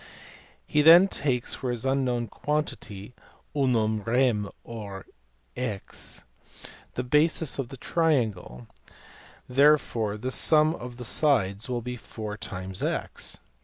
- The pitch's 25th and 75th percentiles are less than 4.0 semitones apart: No, average, 4.8 semitones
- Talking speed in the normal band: No, slow, 115 wpm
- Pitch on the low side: Yes, low, 125 Hz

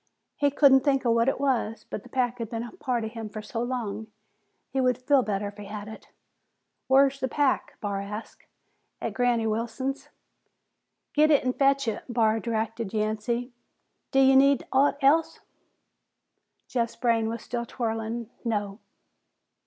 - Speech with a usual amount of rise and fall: Yes, average, 3.2 semitones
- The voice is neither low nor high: No, high, 235 Hz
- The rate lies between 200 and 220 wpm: No, average, 165 wpm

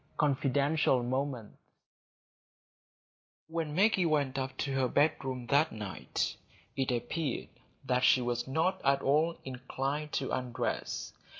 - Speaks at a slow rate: Yes, slow, 115 wpm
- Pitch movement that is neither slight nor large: Yes, average, 3.0 semitones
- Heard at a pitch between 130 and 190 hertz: Yes, low, 135 Hz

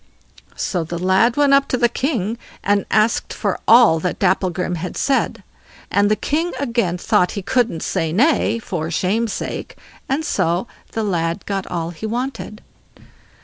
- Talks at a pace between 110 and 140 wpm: No, average, 160 wpm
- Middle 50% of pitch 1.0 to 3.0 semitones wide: No, average, 5.1 semitones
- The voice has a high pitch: Yes, high, 205 Hz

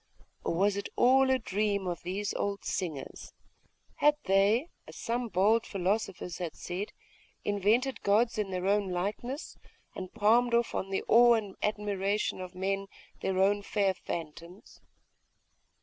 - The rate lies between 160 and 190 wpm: No, average, 145 wpm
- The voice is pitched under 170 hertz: No, high, 200 Hz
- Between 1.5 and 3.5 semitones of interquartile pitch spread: Yes, average, 2.9 semitones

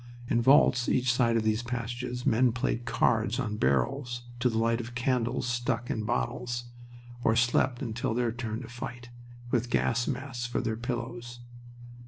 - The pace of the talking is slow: No, average, 165 wpm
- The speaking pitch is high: No, low, 120 Hz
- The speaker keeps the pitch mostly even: Yes, narrow, 1.2 semitones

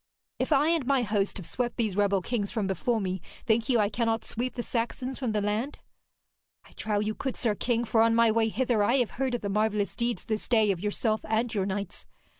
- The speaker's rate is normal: No, fast, 230 wpm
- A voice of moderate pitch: No, high, 225 Hz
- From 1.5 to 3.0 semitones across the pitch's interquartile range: Yes, average, 2.7 semitones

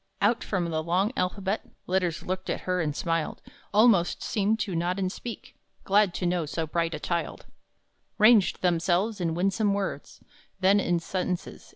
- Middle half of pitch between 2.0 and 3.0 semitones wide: Yes, narrow, 2.6 semitones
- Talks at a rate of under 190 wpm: Yes, average, 165 wpm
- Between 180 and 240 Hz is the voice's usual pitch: Yes, medium, 185 Hz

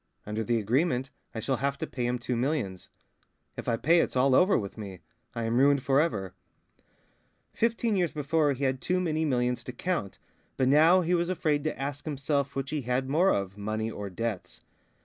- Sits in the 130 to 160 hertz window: Yes, low, 135 Hz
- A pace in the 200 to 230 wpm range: Yes, fast, 205 wpm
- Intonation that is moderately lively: Yes, average, 5.0 semitones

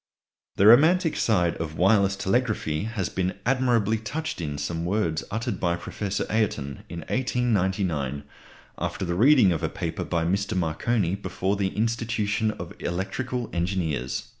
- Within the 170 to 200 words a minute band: No, average, 140 wpm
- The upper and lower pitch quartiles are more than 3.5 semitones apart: Yes, average, 4.8 semitones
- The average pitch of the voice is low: Yes, very low, 95 Hz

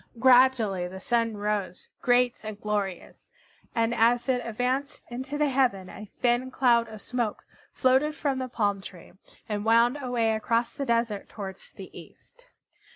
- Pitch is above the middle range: Yes, high, 235 Hz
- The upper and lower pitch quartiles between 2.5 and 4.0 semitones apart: Yes, average, 3.4 semitones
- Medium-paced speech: Yes, average, 155 wpm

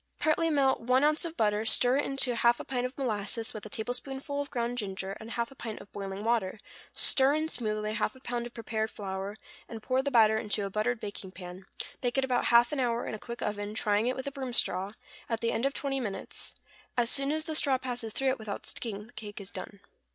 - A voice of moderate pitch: No, high, 235 Hz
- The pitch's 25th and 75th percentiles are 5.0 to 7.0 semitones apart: No, average, 3.8 semitones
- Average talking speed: No, fast, 245 wpm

